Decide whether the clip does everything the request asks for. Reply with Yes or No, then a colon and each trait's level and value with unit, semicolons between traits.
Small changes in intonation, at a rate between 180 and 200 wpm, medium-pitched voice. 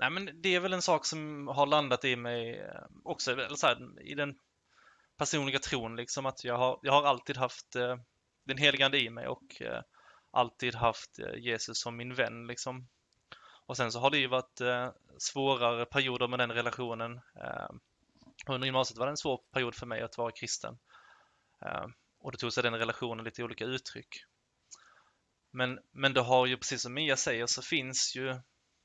No: narrow, 2.3 semitones; average, 190 wpm; low, 125 Hz